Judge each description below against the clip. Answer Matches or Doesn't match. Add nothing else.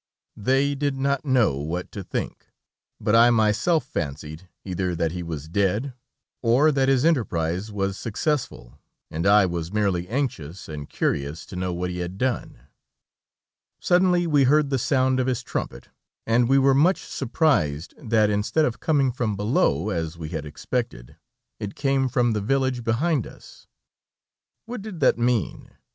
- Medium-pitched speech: Doesn't match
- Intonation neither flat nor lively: Doesn't match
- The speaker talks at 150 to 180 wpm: Matches